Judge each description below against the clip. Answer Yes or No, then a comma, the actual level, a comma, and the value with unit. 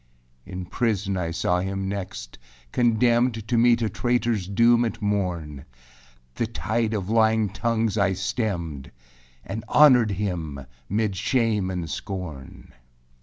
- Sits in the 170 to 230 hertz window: No, low, 105 Hz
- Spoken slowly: Yes, slow, 130 wpm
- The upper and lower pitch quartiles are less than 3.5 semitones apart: No, average, 3.8 semitones